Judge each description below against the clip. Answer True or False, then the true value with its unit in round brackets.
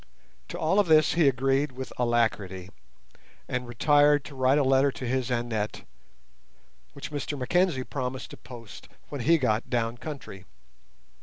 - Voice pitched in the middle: False (130 Hz)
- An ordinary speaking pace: True (150 wpm)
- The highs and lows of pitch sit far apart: False (3.5 semitones)